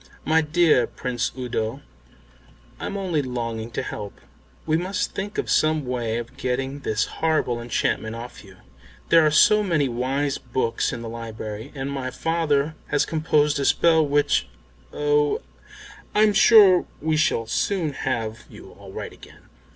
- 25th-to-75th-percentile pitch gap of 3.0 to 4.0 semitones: No, average, 5.1 semitones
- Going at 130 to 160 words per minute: Yes, average, 150 wpm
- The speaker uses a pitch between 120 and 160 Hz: Yes, medium, 140 Hz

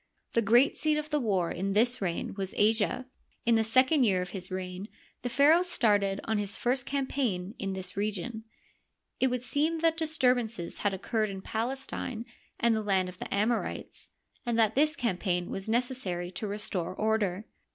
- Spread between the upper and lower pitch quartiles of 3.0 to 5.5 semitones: Yes, average, 4.5 semitones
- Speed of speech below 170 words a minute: No, average, 175 wpm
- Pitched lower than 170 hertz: No, high, 220 Hz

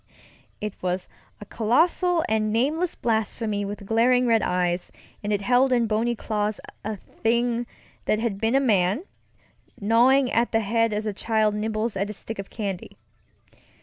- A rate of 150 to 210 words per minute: Yes, average, 160 wpm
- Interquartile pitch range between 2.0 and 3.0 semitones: Yes, narrow, 2.5 semitones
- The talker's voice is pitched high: Yes, high, 220 Hz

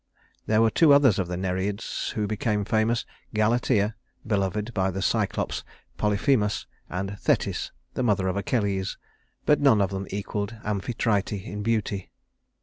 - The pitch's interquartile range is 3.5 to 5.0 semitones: No, narrow, 2.4 semitones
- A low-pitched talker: Yes, low, 105 Hz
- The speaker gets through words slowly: No, average, 145 wpm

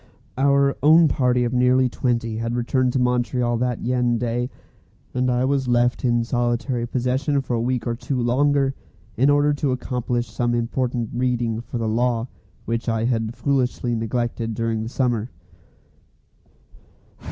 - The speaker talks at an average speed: Yes, average, 150 wpm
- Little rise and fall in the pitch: Yes, narrow, 1.5 semitones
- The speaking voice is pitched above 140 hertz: No, low, 125 Hz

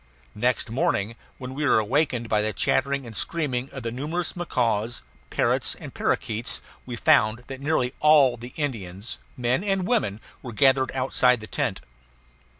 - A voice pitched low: Yes, low, 125 Hz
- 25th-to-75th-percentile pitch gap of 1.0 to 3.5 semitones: No, average, 3.9 semitones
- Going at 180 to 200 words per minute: No, average, 155 wpm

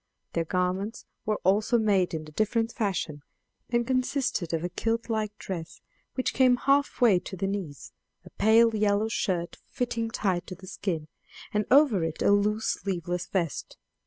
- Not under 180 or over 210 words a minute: No, average, 165 wpm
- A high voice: Yes, high, 205 Hz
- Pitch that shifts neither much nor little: Yes, average, 4.2 semitones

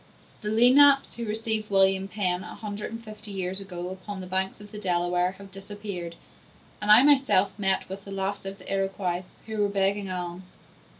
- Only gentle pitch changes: Yes, narrow, 2.1 semitones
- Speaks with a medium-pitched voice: No, high, 195 Hz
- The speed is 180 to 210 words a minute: Yes, average, 185 wpm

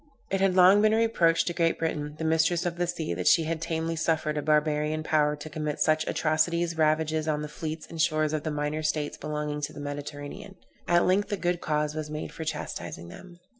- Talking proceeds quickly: Yes, fast, 215 wpm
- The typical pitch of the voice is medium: Yes, medium, 155 Hz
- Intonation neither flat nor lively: No, narrow, 1.9 semitones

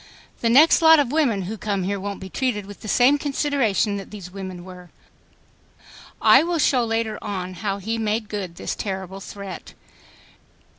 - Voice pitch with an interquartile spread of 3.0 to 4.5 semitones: Yes, average, 4.2 semitones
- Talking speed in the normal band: Yes, average, 170 wpm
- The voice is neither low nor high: No, high, 210 Hz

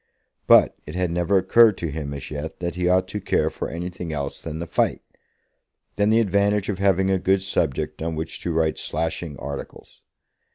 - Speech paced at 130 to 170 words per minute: No, average, 195 wpm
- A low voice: Yes, very low, 90 Hz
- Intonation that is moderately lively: Yes, average, 3.4 semitones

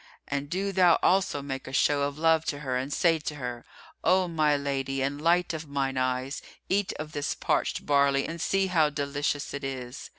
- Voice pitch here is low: No, medium, 145 Hz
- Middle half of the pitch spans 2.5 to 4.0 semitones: Yes, average, 3.1 semitones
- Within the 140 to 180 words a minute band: No, average, 200 wpm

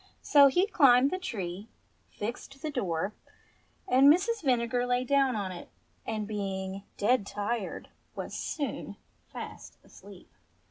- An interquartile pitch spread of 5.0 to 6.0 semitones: Yes, wide, 5.4 semitones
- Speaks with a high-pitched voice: Yes, high, 245 Hz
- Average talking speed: No, slow, 130 wpm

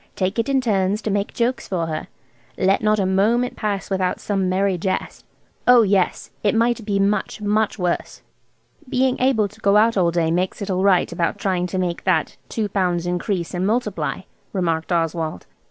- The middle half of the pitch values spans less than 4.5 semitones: Yes, average, 3.0 semitones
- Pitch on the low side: No, high, 195 Hz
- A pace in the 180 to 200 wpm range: Yes, average, 185 wpm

